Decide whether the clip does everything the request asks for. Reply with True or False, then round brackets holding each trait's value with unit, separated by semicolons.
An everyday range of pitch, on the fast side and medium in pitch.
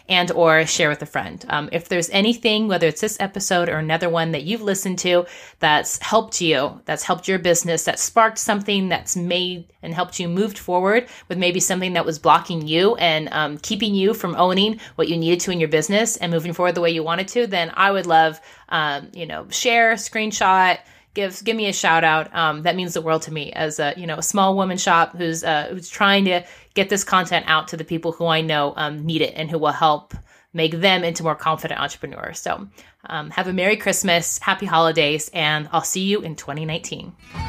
True (3.3 semitones; 220 wpm; 175 Hz)